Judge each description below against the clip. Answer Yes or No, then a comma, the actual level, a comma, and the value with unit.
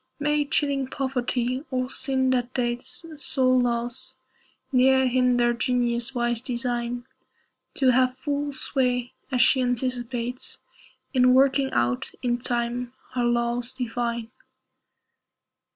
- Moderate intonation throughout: No, narrow, 1.5 semitones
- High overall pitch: Yes, very high, 250 Hz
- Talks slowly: Yes, slow, 110 wpm